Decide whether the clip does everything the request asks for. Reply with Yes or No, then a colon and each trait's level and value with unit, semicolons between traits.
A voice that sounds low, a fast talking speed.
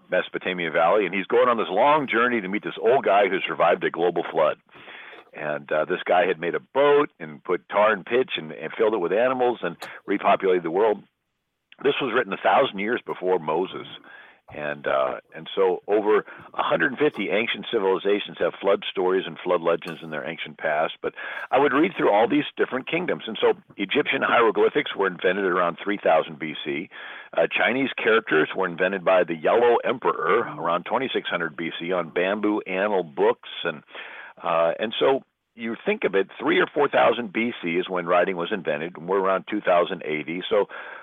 No: low, 130 Hz; average, 185 wpm